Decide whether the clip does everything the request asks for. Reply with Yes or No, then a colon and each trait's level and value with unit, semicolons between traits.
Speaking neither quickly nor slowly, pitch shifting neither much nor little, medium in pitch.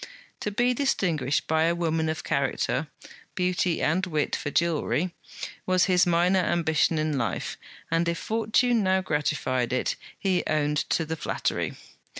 Yes: average, 150 wpm; average, 3.3 semitones; medium, 170 Hz